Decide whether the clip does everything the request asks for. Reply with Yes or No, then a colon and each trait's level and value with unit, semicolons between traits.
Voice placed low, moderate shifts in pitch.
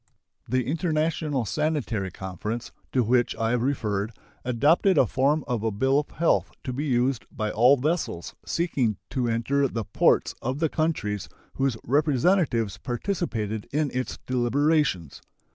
Yes: low, 130 Hz; average, 4.7 semitones